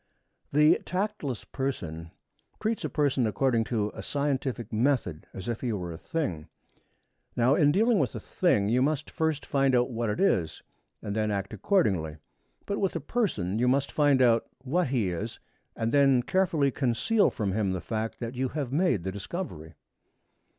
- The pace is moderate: Yes, average, 180 wpm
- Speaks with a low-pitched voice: Yes, low, 125 Hz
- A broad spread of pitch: Yes, wide, 6.1 semitones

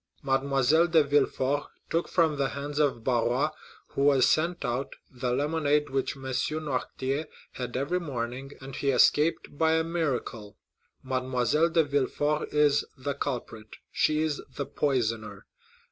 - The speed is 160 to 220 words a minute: No, average, 140 wpm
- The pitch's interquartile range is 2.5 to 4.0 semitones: Yes, average, 2.8 semitones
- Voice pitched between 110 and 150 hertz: Yes, medium, 140 Hz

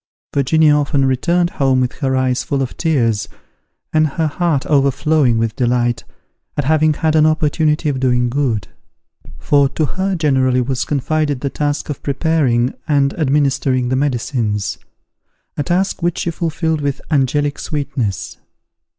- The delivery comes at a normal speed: Yes, average, 145 wpm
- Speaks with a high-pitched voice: No, medium, 140 Hz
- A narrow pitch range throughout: No, average, 3.3 semitones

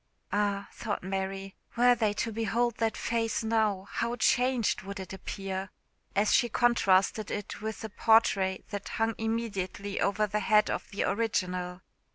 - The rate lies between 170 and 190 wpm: No, average, 155 wpm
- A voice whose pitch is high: Yes, high, 210 Hz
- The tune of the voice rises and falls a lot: No, narrow, 2.6 semitones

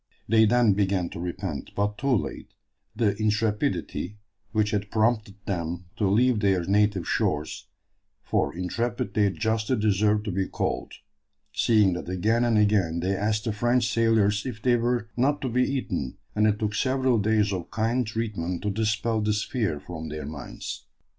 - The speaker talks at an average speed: Yes, average, 165 wpm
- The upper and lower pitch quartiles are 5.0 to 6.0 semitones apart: No, average, 2.9 semitones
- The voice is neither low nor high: No, low, 105 Hz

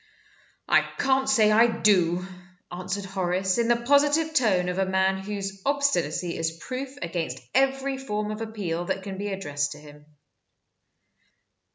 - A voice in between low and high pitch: No, high, 195 Hz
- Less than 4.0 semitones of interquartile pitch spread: No, average, 5.1 semitones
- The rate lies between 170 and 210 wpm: No, average, 150 wpm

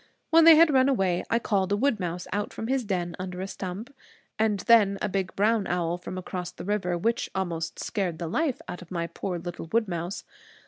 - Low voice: No, high, 190 Hz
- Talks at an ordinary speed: No, fast, 220 wpm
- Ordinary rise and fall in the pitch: Yes, average, 4.1 semitones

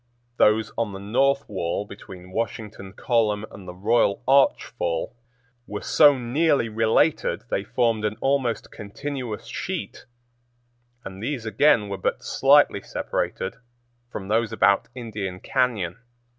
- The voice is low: Yes, low, 110 Hz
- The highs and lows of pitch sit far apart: No, average, 3.6 semitones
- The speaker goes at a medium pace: No, slow, 130 wpm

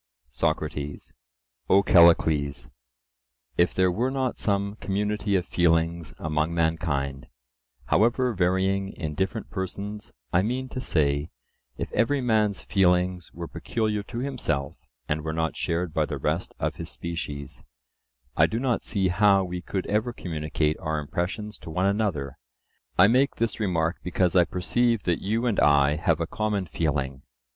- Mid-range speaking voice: No, very low, 90 Hz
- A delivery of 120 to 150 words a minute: Yes, average, 145 wpm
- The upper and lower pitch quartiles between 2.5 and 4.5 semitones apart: No, average, 5.0 semitones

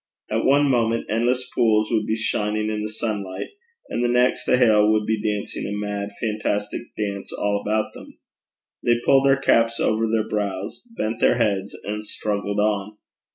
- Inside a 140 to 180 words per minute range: Yes, average, 175 wpm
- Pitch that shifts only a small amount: Yes, narrow, 1.9 semitones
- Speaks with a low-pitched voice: Yes, low, 110 Hz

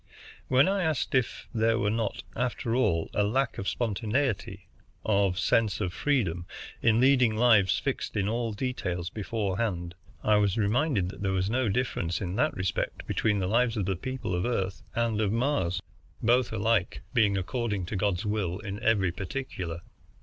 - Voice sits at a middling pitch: No, low, 105 Hz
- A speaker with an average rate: Yes, average, 170 wpm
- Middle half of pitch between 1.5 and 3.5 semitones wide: No, average, 4.0 semitones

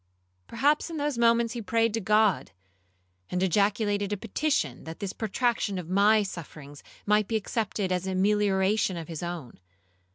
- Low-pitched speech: No, high, 205 Hz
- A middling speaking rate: Yes, average, 160 wpm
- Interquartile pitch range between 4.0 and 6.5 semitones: No, average, 3.5 semitones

